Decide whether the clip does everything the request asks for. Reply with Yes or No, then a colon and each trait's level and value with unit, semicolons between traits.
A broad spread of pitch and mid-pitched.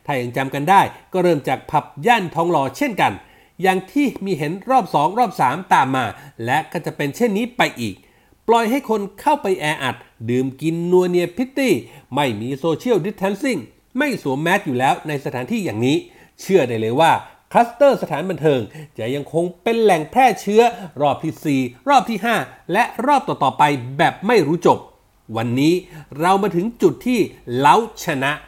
Yes: wide, 8.0 semitones; medium, 175 Hz